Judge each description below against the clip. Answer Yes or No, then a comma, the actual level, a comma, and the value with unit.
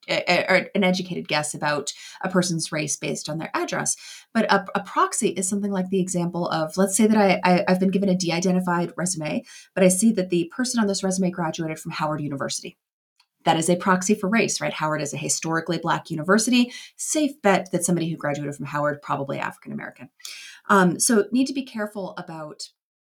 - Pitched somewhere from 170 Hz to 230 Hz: Yes, medium, 185 Hz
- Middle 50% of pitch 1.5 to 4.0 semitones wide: Yes, average, 3.7 semitones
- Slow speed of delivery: No, average, 200 wpm